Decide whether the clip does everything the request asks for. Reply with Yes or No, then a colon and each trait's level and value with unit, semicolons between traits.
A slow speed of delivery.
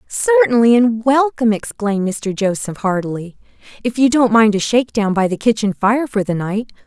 No: average, 175 wpm